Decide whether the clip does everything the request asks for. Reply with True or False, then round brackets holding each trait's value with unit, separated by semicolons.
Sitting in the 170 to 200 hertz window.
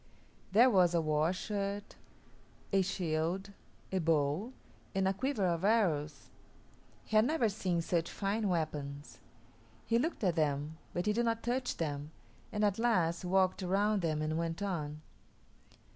True (185 Hz)